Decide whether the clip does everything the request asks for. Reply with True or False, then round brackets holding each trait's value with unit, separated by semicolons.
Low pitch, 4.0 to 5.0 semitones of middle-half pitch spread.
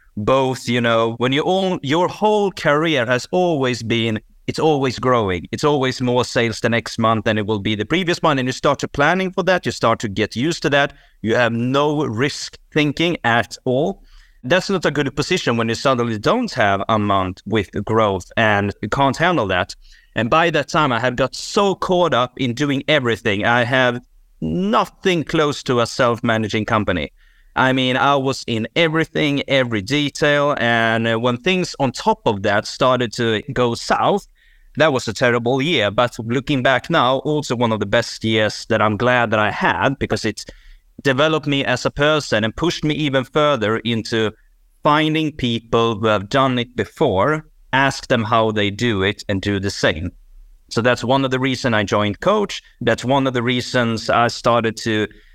True (125 Hz; 4.5 semitones)